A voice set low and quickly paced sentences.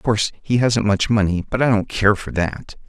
Yes: low, 105 Hz; fast, 250 wpm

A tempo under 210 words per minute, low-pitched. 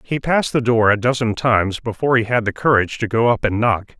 No: fast, 255 wpm; low, 115 Hz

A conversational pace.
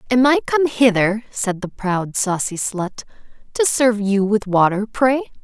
Yes: average, 165 wpm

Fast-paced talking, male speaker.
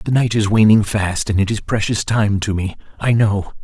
Yes: fast, 230 wpm; male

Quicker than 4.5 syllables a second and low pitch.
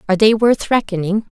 No: 6.2 syllables/s; high, 210 Hz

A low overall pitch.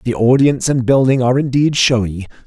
Yes: low, 125 Hz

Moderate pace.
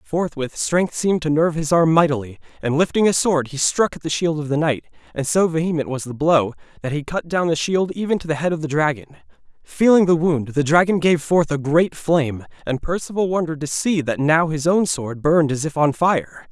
No: fast, 235 wpm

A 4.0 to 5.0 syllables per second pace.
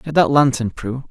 Yes: 4.7 syllables/s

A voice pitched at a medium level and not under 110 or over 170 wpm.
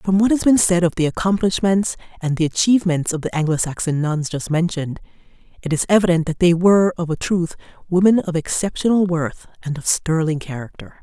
No: medium, 170 Hz; average, 185 wpm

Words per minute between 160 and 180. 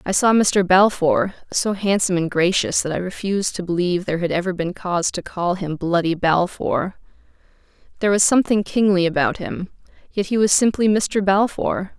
Yes: average, 170 wpm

